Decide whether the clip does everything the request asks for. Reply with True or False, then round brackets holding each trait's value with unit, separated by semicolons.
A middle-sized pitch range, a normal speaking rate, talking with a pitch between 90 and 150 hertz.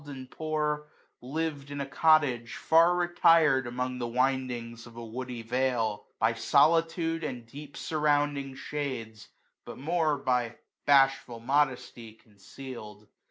False (4.0 semitones; 115 wpm; 135 Hz)